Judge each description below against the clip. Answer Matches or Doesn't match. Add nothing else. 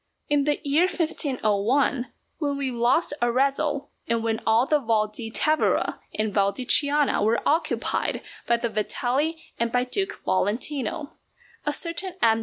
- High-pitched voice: Matches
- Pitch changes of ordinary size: Matches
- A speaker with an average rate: Matches